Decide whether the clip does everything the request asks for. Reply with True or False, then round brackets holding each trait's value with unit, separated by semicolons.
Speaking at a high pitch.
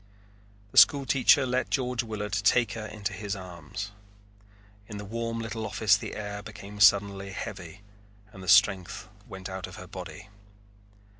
False (105 Hz)